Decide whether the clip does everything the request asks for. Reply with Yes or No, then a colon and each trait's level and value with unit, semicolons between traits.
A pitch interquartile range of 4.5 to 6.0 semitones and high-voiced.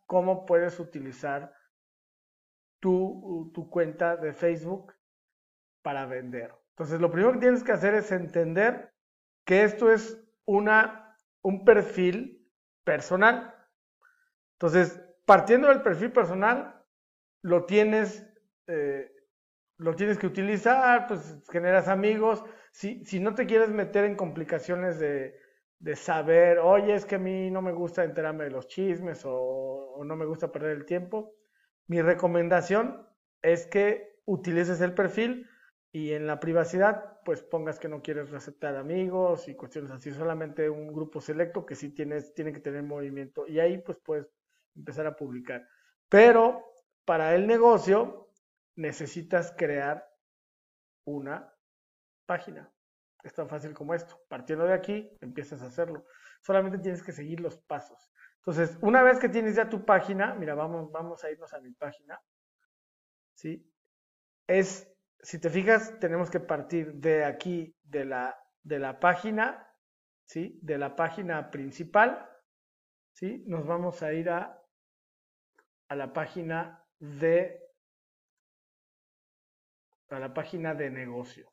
No: average, 5.1 semitones; medium, 175 Hz